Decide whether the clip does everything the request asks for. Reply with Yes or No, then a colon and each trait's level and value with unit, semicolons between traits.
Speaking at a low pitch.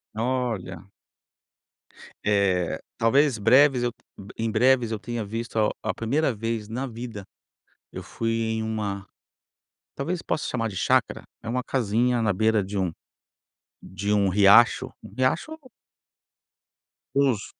Yes: low, 115 Hz